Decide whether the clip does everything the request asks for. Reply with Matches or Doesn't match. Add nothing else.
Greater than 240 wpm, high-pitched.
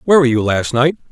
Doesn't match